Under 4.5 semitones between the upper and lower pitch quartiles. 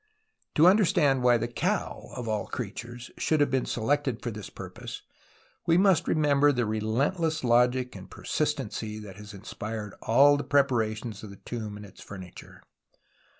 No: average, 4.8 semitones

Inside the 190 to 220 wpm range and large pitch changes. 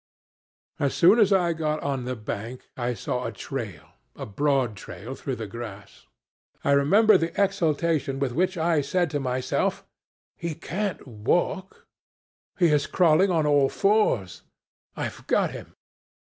No: average, 145 wpm; wide, 5.7 semitones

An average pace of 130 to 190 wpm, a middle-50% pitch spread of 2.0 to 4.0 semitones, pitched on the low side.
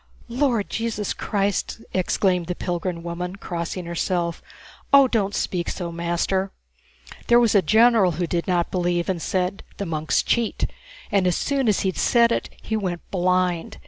No: average, 160 wpm; average, 3.5 semitones; medium, 185 Hz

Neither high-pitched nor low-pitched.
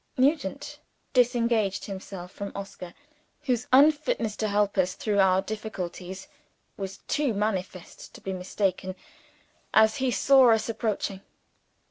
No: high, 210 Hz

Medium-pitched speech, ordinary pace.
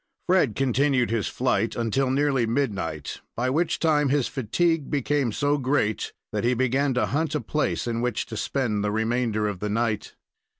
No: low, 125 Hz; average, 175 wpm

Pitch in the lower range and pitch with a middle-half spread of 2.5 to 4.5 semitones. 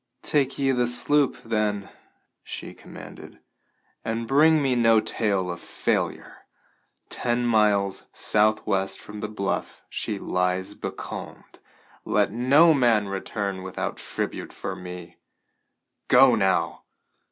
Yes: low, 110 Hz; average, 4.0 semitones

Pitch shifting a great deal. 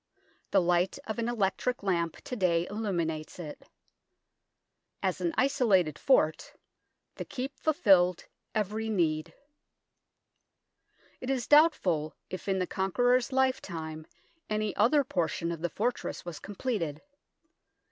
Yes: wide, 6.4 semitones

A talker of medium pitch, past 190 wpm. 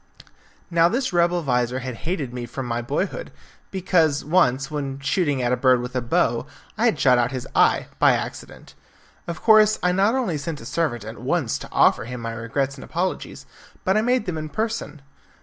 Yes: medium, 145 Hz; average, 200 wpm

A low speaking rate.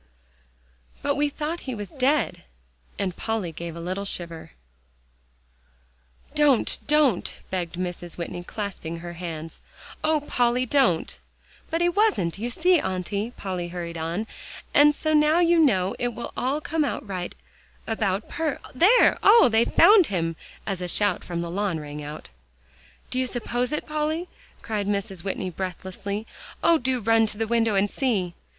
No: average, 155 wpm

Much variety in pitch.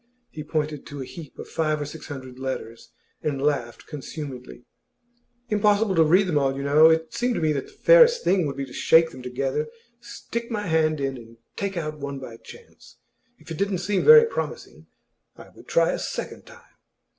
Yes: wide, 6.2 semitones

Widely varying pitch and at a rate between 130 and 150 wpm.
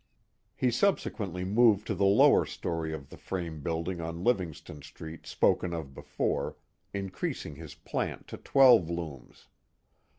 No: average, 3.8 semitones; average, 140 wpm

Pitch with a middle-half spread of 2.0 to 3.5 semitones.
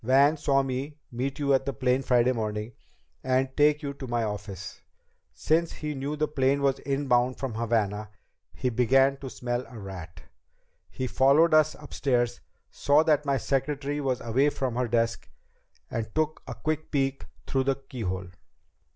Yes: average, 3.0 semitones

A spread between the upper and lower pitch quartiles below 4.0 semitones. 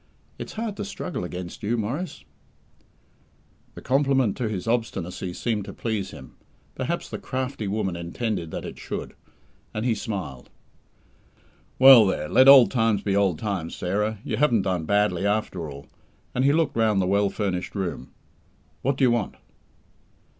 No: average, 5.0 semitones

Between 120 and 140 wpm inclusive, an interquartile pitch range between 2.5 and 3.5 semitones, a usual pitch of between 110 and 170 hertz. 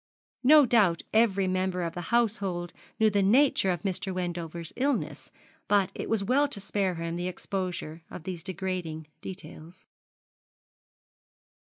No: slow, 135 wpm; average, 2.9 semitones; medium, 185 Hz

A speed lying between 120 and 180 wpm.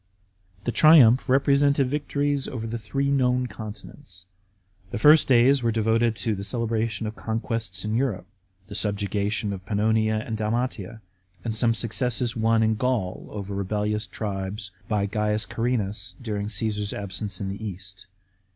Yes: average, 145 wpm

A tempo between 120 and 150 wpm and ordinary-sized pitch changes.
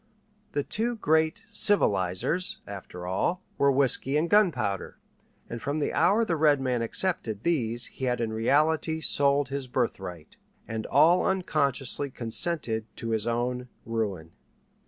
No: slow, 135 wpm; wide, 5.9 semitones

